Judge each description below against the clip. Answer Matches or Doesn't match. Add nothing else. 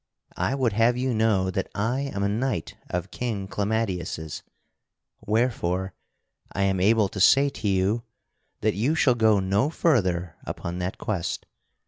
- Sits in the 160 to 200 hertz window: Doesn't match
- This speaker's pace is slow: Doesn't match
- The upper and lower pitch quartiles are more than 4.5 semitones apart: Doesn't match